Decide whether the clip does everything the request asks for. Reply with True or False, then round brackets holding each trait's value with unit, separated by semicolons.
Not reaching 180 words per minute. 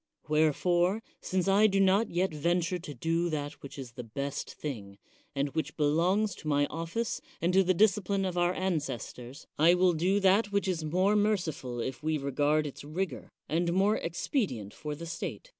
False (185 wpm)